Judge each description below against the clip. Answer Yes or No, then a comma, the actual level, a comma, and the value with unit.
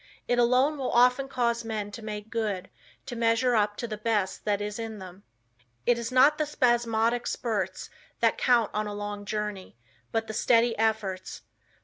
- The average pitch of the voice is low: No, high, 225 Hz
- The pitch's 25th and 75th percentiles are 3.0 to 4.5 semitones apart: No, narrow, 2.6 semitones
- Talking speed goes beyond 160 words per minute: Yes, average, 180 wpm